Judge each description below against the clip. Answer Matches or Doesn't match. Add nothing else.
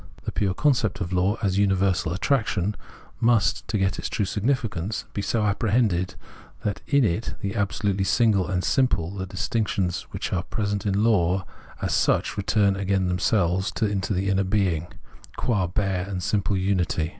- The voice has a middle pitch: Doesn't match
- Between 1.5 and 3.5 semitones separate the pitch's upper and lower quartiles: Matches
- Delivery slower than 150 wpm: Doesn't match